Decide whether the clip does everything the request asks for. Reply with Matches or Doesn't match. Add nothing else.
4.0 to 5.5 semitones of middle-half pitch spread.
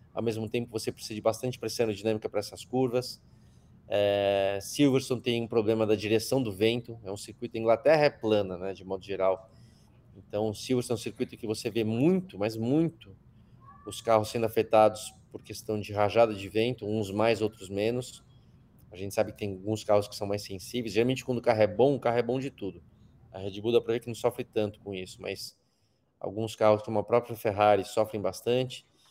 Doesn't match